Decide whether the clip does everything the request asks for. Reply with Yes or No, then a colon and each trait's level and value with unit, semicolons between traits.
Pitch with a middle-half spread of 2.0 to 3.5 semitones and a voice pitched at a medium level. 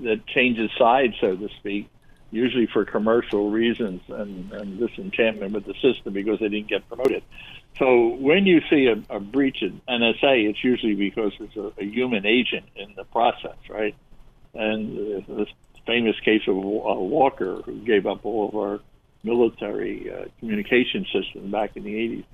No: average, 2.9 semitones; low, 110 Hz